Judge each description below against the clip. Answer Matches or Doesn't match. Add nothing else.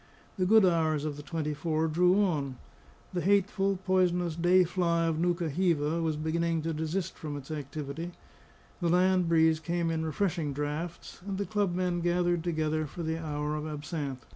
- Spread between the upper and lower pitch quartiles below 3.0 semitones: Matches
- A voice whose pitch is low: Doesn't match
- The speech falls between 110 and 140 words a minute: Doesn't match